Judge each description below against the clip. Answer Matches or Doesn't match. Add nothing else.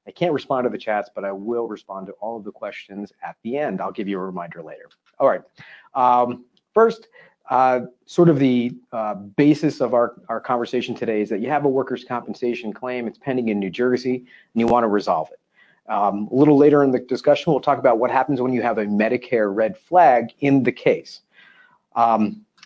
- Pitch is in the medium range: Doesn't match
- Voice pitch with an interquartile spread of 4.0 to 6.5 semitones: Doesn't match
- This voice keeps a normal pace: Doesn't match